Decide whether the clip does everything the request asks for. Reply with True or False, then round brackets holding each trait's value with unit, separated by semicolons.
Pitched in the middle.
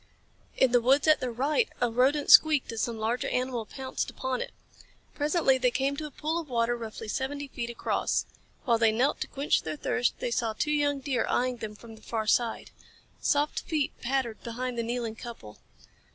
False (250 Hz)